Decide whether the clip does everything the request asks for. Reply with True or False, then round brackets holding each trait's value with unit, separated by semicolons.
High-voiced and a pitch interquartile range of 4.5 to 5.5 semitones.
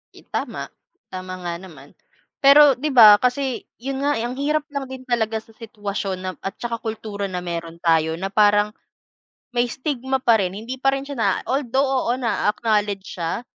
True (225 Hz; 5.1 semitones)